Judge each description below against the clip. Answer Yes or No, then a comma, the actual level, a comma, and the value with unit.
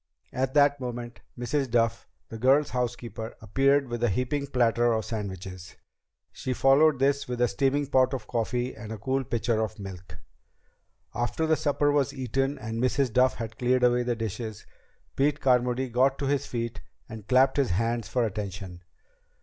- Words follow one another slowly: No, average, 170 wpm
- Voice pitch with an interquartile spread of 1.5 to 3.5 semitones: Yes, average, 3.1 semitones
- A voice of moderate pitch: No, low, 125 Hz